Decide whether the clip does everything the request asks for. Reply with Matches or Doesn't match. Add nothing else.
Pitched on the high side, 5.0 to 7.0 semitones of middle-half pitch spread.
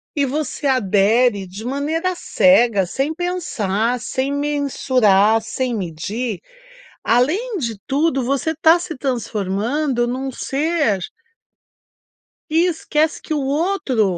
Matches